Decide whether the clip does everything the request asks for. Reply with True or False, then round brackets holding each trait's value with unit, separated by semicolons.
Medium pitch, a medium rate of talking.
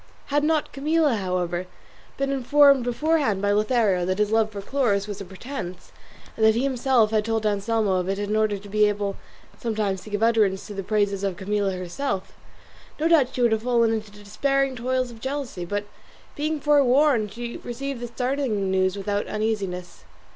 False (220 Hz; 185 wpm)